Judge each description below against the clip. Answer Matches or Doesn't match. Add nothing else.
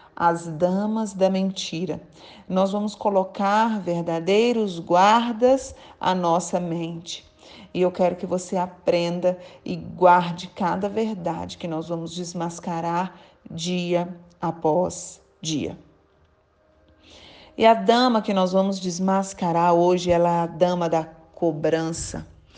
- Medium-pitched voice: Matches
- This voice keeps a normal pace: Doesn't match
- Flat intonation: Matches